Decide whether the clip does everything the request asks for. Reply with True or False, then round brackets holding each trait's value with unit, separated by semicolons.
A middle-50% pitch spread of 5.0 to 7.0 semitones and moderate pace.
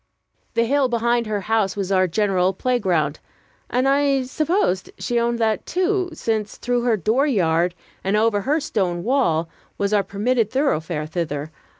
True (5.4 semitones; 155 wpm)